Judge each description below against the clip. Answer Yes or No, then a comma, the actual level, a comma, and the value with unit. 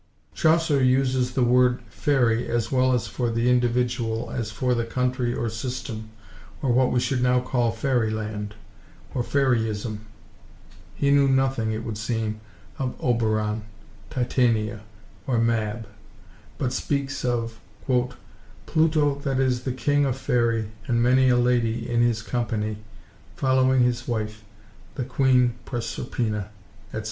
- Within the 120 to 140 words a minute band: Yes, slow, 135 wpm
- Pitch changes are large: No, narrow, 2.4 semitones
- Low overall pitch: Yes, low, 120 Hz